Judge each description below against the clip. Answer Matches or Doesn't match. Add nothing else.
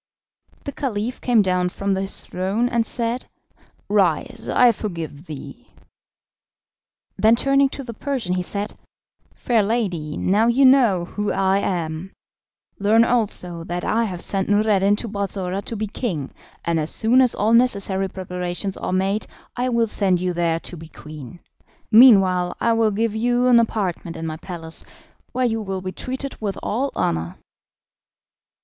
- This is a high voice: Matches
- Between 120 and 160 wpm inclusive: Matches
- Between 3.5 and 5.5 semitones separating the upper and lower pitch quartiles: Matches